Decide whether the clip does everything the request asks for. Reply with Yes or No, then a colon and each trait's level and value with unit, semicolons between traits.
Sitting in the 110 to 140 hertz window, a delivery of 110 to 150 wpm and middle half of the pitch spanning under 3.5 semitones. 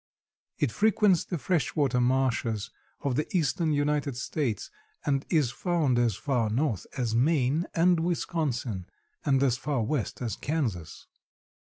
No: low, 135 Hz; average, 140 wpm; average, 4.6 semitones